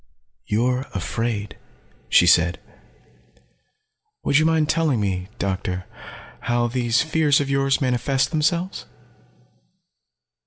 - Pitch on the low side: Yes, low, 125 Hz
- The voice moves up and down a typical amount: No, wide, 6.0 semitones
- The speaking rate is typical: No, slow, 95 wpm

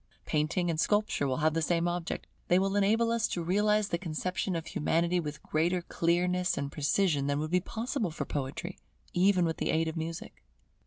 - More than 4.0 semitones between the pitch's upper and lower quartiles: No, average, 3.2 semitones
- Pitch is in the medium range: Yes, medium, 175 Hz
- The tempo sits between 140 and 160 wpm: No, average, 195 wpm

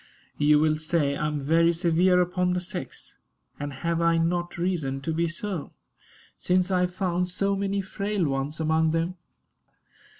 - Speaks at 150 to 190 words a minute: Yes, average, 165 wpm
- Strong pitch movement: No, narrow, 2.5 semitones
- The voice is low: No, medium, 170 Hz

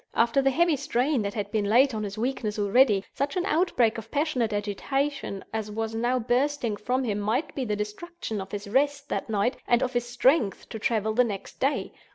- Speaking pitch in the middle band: No, high, 235 Hz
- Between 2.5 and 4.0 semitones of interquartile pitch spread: No, average, 4.4 semitones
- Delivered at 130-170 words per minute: No, fast, 205 wpm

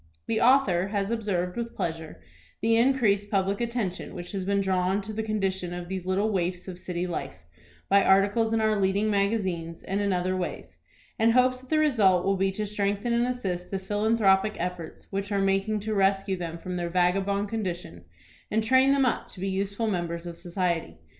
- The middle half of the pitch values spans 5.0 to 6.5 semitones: No, average, 3.1 semitones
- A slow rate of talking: No, average, 195 wpm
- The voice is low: No, high, 195 Hz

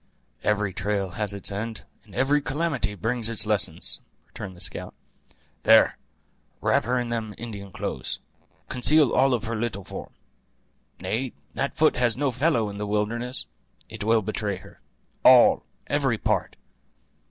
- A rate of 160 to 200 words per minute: No, average, 150 wpm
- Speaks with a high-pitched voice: No, low, 110 Hz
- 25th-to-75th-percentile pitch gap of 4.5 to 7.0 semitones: No, average, 3.4 semitones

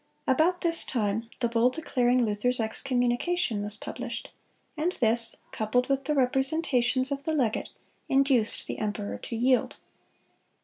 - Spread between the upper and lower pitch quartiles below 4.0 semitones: Yes, average, 3.3 semitones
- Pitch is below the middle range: No, very high, 250 Hz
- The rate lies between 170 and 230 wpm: No, slow, 135 wpm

